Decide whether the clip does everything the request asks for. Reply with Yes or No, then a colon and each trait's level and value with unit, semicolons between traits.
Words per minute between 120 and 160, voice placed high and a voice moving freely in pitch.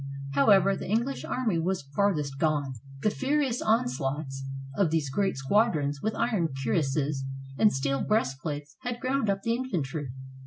No: average, 145 wpm; medium, 165 Hz; wide, 7.9 semitones